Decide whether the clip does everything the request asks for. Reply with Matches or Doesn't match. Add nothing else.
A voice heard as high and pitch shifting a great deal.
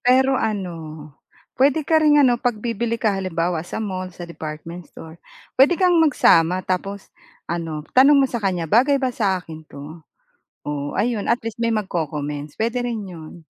Matches